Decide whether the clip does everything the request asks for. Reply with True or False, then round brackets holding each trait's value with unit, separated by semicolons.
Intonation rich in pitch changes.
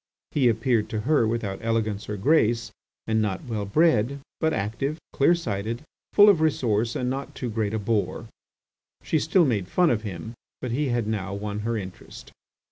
False (4.6 semitones)